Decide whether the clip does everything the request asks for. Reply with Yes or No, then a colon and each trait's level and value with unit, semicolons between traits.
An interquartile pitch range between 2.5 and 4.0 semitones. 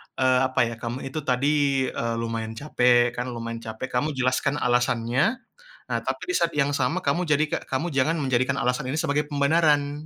Yes: average, 3.2 semitones